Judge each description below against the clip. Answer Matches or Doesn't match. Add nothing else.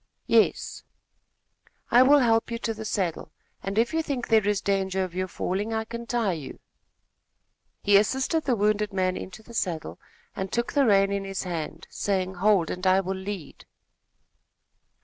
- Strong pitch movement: Doesn't match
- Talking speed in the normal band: Matches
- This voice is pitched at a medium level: Doesn't match